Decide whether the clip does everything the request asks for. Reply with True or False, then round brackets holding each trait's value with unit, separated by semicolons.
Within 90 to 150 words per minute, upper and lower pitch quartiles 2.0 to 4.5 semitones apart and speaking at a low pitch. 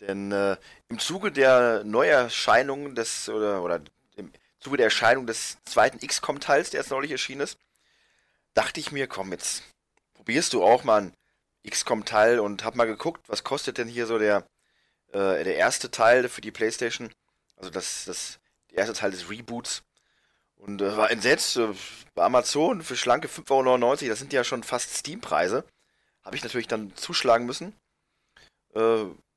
False (165 wpm; 3.3 semitones; 115 Hz)